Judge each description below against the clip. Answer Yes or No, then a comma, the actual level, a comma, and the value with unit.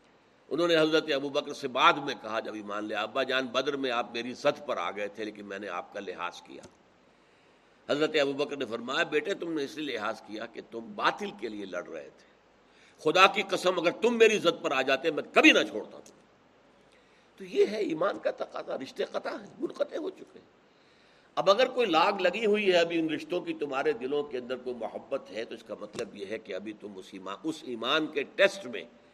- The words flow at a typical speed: No, fast, 225 wpm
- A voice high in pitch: No, medium, 145 Hz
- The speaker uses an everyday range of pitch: No, wide, 7.1 semitones